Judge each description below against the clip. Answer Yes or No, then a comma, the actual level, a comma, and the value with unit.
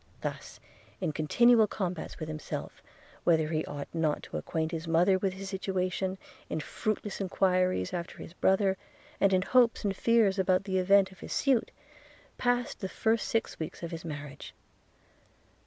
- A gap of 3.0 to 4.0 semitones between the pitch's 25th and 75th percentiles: Yes, average, 3.5 semitones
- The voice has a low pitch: No, medium, 185 Hz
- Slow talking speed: No, average, 160 wpm